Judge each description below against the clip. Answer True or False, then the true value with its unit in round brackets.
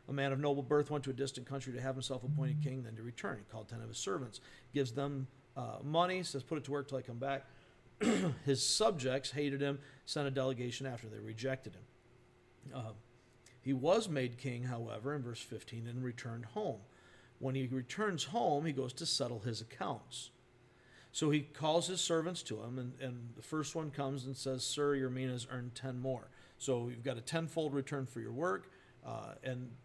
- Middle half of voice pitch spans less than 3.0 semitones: True (2.5 semitones)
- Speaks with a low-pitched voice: True (130 Hz)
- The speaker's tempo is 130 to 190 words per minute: False (205 wpm)